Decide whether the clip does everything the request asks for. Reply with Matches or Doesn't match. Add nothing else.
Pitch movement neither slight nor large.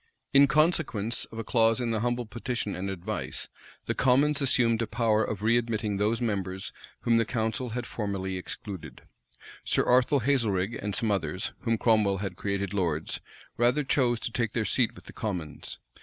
Matches